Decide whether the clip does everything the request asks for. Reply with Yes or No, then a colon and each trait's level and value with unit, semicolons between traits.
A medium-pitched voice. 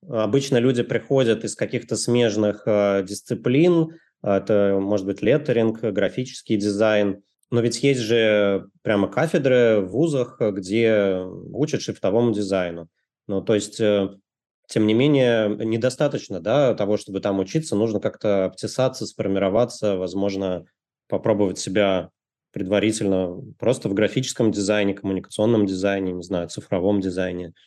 No: low, 105 Hz